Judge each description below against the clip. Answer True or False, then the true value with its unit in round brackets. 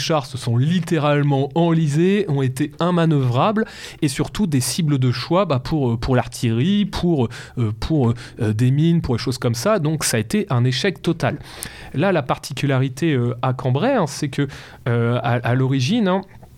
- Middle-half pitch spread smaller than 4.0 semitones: False (5.0 semitones)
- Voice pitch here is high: False (140 Hz)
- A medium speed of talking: True (180 wpm)